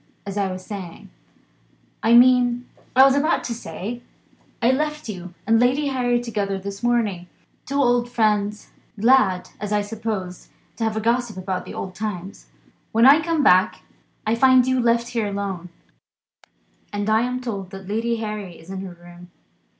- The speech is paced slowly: No, average, 170 wpm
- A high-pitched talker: Yes, high, 220 Hz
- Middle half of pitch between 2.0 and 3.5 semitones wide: No, average, 4.0 semitones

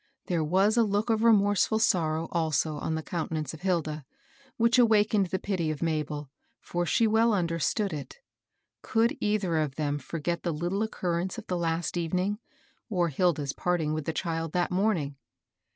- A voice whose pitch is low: No, medium, 175 Hz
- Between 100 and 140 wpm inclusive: No, average, 170 wpm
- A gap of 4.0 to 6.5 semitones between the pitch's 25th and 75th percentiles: Yes, average, 4.5 semitones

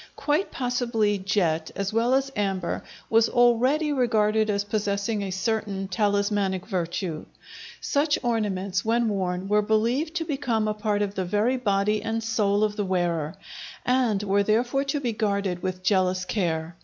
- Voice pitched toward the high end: Yes, high, 210 Hz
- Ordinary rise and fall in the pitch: Yes, average, 3.4 semitones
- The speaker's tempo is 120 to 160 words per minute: Yes, average, 155 wpm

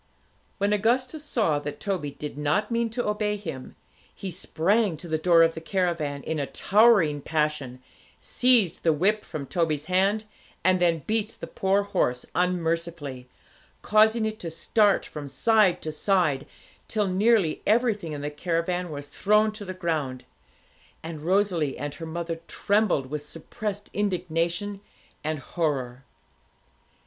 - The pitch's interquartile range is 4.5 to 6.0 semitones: Yes, wide, 5.4 semitones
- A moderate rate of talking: Yes, average, 145 wpm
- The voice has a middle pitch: Yes, medium, 175 Hz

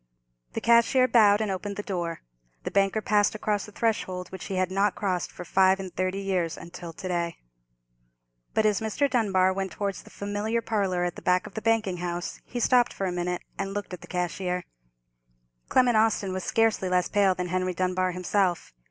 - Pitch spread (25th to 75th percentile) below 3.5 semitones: Yes, narrow, 2.5 semitones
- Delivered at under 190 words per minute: No, average, 195 wpm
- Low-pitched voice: No, high, 190 Hz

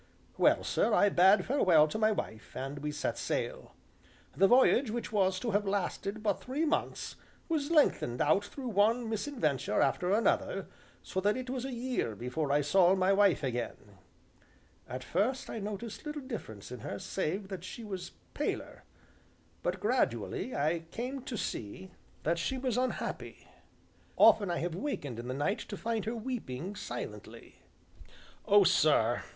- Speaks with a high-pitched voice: Yes, high, 195 Hz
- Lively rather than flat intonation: Yes, wide, 7.3 semitones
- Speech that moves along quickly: No, average, 160 wpm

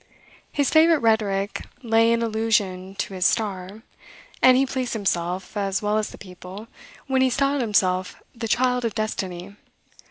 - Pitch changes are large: No, average, 3.9 semitones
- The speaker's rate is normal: Yes, average, 155 wpm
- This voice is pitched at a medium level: No, high, 215 Hz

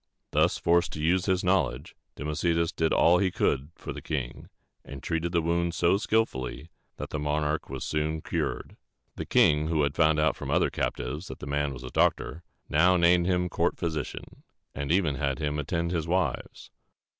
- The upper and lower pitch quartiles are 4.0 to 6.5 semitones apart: No, average, 2.8 semitones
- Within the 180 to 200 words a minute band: Yes, average, 190 wpm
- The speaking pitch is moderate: No, very low, 80 Hz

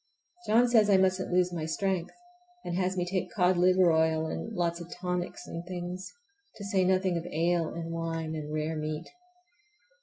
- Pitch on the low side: No, medium, 175 Hz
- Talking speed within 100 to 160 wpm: No, average, 180 wpm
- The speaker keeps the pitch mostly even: Yes, narrow, 2.1 semitones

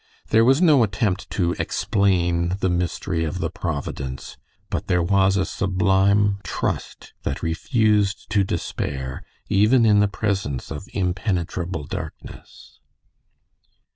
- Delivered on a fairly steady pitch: No, average, 3.1 semitones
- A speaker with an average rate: No, slow, 120 wpm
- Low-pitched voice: Yes, very low, 95 Hz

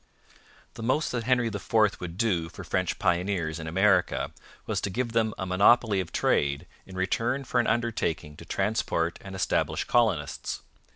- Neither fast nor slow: Yes, average, 165 wpm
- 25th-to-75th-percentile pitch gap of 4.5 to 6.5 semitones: Yes, average, 4.8 semitones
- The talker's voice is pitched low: Yes, low, 100 Hz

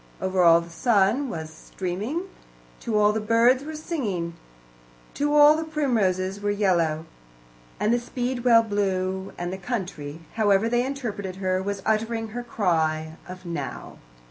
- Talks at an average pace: Yes, average, 145 wpm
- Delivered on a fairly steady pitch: No, average, 4.7 semitones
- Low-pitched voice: No, high, 205 Hz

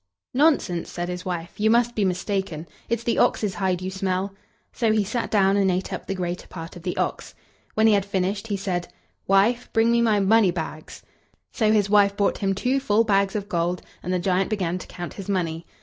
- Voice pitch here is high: Yes, high, 195 Hz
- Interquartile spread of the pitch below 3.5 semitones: Yes, average, 2.9 semitones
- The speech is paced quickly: Yes, fast, 215 wpm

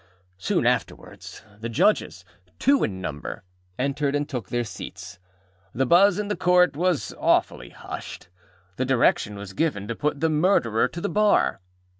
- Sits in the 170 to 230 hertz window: No, medium, 140 Hz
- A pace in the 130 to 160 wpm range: Yes, average, 155 wpm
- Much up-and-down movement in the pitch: Yes, wide, 8.1 semitones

